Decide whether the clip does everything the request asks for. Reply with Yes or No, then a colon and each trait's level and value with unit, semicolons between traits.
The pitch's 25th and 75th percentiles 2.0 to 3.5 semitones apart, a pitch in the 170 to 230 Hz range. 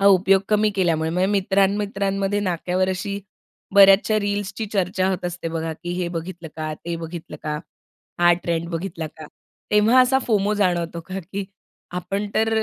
Yes: average, 2.9 semitones; high, 190 Hz